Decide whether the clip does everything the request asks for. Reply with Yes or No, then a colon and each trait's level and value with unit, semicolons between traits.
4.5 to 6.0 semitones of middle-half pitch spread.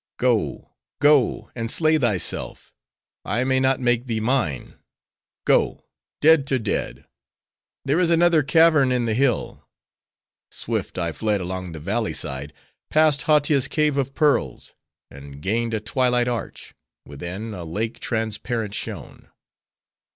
Yes: average, 5.1 semitones